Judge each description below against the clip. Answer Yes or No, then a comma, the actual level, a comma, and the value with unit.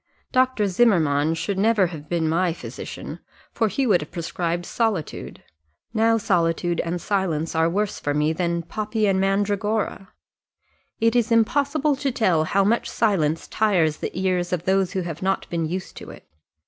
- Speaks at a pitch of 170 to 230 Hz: Yes, high, 190 Hz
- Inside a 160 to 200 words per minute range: Yes, average, 165 wpm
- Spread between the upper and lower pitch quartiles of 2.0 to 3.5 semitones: No, average, 4.5 semitones